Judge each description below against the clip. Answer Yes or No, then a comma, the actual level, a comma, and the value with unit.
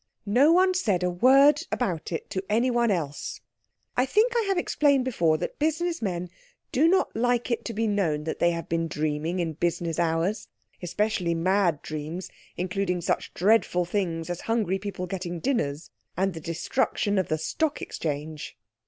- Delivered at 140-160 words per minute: No, average, 170 wpm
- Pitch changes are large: Yes, wide, 6.4 semitones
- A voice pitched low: No, medium, 185 Hz